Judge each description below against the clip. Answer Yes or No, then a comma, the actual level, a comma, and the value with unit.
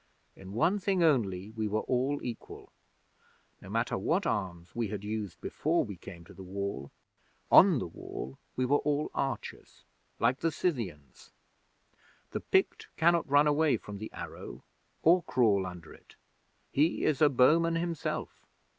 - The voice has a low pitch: Yes, low, 125 Hz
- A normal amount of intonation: No, wide, 7.5 semitones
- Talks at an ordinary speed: Yes, average, 155 wpm